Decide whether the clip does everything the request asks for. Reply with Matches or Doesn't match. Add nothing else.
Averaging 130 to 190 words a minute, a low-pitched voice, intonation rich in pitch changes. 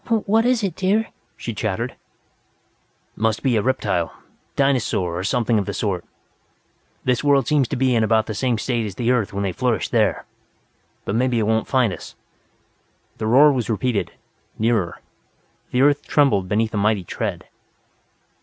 Doesn't match